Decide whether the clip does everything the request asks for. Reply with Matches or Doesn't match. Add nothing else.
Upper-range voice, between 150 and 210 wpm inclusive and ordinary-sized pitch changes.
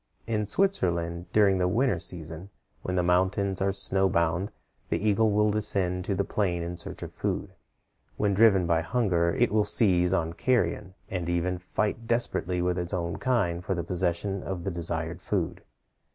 Doesn't match